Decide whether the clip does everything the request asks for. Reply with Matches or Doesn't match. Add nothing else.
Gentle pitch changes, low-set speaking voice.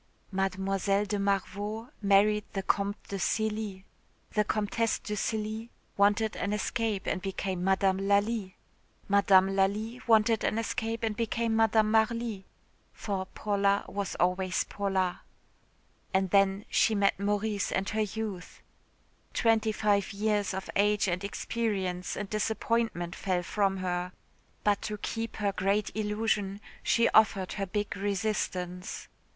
Doesn't match